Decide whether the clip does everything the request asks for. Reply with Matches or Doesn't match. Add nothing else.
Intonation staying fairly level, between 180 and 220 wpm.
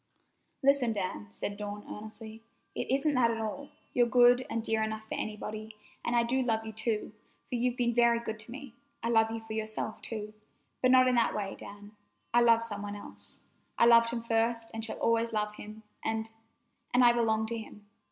Matches